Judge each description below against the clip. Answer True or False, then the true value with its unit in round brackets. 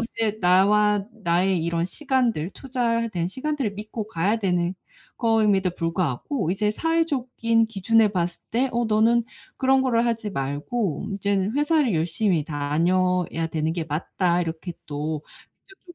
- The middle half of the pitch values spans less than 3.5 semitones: False (5.2 semitones)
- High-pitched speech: True (200 Hz)